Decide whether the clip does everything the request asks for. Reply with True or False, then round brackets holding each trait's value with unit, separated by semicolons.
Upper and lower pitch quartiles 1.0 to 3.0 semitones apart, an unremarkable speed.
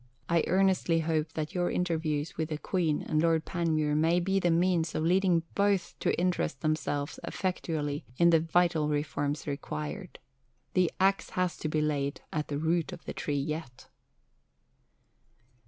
True (2.7 semitones; 155 wpm)